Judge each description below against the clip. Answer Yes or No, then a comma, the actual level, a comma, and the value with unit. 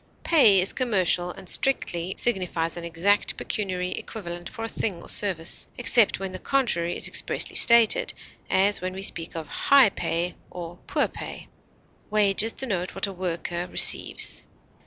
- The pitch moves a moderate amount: Yes, average, 3.4 semitones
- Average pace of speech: Yes, average, 155 wpm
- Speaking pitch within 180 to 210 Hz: Yes, medium, 185 Hz